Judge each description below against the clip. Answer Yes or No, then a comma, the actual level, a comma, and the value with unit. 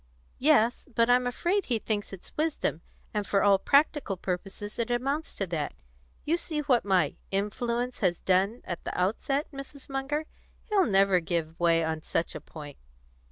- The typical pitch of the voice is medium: No, high, 215 Hz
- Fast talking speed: No, average, 165 wpm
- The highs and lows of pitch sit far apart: Yes, wide, 7.0 semitones